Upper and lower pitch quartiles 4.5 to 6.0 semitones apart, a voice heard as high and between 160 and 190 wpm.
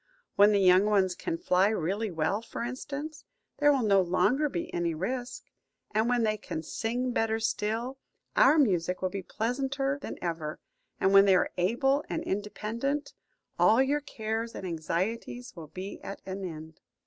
Yes: average, 5.3 semitones; high, 215 Hz; average, 170 wpm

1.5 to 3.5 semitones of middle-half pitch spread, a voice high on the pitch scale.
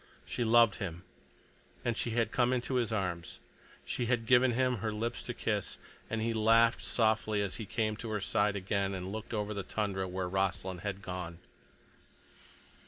No: average, 3.1 semitones; low, 110 Hz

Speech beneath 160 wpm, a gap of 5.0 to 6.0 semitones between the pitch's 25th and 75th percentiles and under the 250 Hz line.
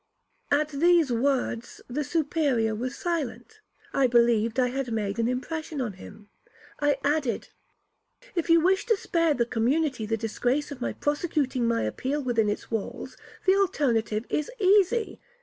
No: average, 150 wpm; average, 5.3 semitones; very high, 270 Hz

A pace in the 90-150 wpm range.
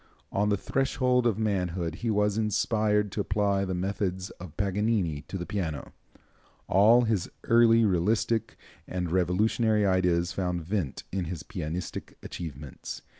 Yes: slow, 135 wpm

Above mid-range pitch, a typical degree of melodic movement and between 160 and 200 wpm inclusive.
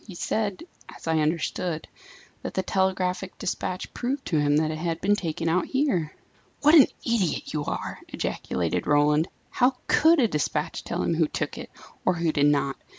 No: medium, 170 Hz; average, 4.9 semitones; average, 180 wpm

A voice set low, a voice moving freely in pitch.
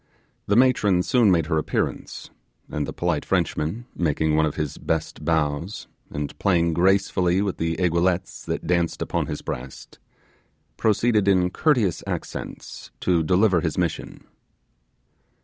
No: very low, 90 Hz; average, 3.5 semitones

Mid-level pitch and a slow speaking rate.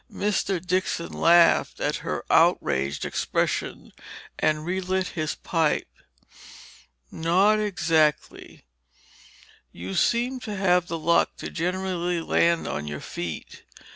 Yes: medium, 170 Hz; slow, 105 wpm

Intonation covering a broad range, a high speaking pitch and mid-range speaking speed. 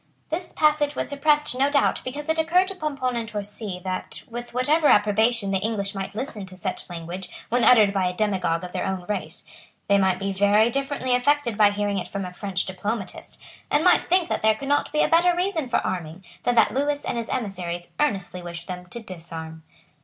No: wide, 7.0 semitones; high, 215 Hz; fast, 210 wpm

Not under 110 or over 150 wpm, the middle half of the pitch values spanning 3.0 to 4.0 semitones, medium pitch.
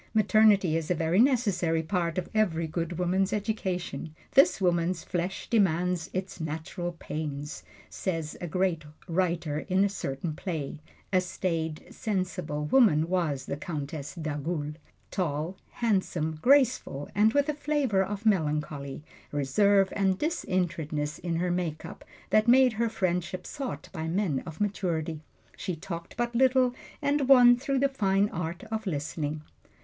No: average, 145 wpm; average, 4.7 semitones; medium, 180 Hz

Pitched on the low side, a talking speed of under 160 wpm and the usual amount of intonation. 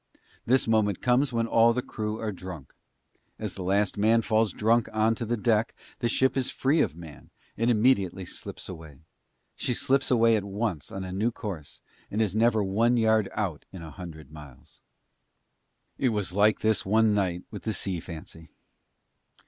No: low, 105 Hz; average, 180 wpm; average, 3.8 semitones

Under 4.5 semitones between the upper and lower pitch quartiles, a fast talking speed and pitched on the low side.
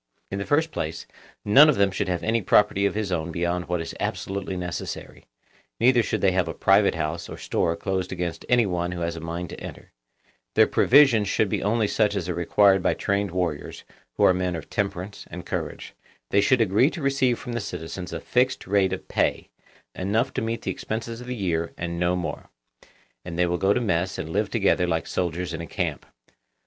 Yes: average, 3.8 semitones; fast, 215 wpm; very low, 95 Hz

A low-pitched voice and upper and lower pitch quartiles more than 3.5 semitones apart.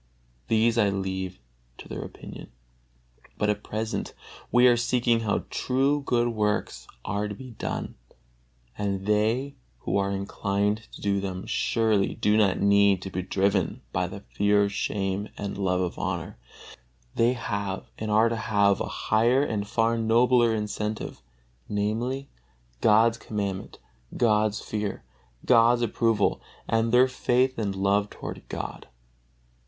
No: low, 105 Hz; narrow, 2.6 semitones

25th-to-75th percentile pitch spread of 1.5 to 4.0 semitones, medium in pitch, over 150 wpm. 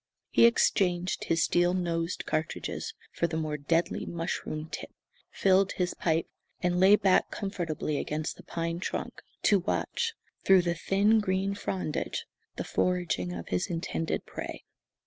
No: average, 2.7 semitones; medium, 175 Hz; average, 145 wpm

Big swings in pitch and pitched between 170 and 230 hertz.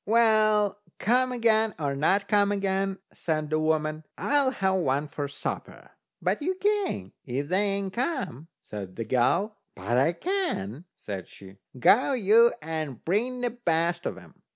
Yes: wide, 7.8 semitones; high, 190 Hz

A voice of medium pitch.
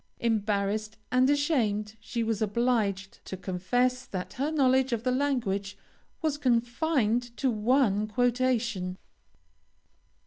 No: high, 235 Hz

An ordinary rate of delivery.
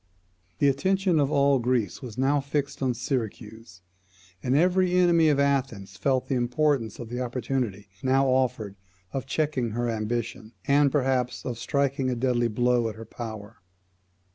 Yes: average, 155 wpm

